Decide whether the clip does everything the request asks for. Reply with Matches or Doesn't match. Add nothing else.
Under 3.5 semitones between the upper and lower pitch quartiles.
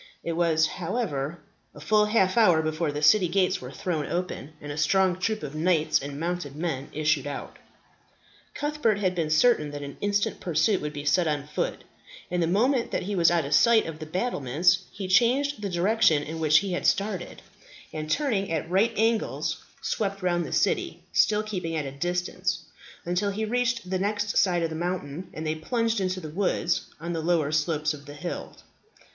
Doesn't match